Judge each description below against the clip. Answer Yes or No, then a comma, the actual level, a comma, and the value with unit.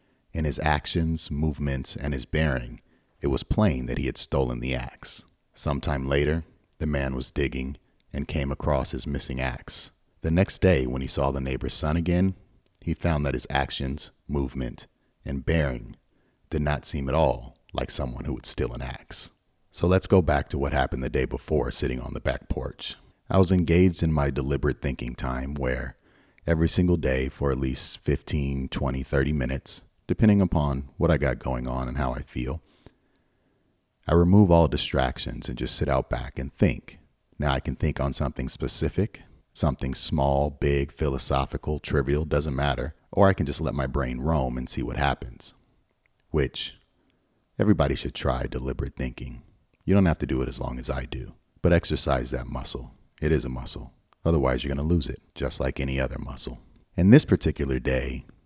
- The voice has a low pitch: Yes, very low, 70 Hz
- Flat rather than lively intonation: No, average, 3.4 semitones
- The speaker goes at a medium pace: Yes, average, 185 wpm